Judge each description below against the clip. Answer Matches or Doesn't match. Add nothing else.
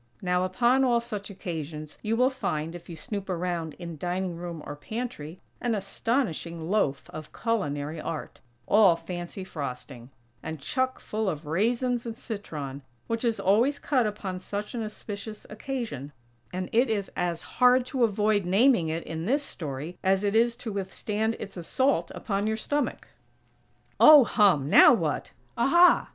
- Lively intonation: Matches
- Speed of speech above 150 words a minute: Matches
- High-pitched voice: Matches